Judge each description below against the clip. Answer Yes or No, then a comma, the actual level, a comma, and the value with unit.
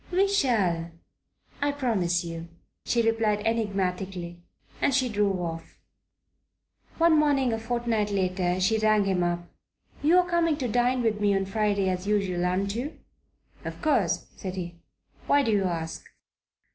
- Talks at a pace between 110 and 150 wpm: Yes, average, 145 wpm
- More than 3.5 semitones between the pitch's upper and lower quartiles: Yes, average, 5.1 semitones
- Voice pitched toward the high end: Yes, high, 210 Hz